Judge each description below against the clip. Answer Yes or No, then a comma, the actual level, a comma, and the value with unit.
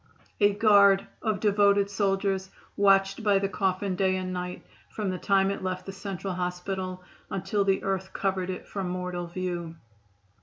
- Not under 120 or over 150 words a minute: No, average, 160 wpm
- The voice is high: Yes, high, 195 Hz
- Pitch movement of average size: No, narrow, 1.5 semitones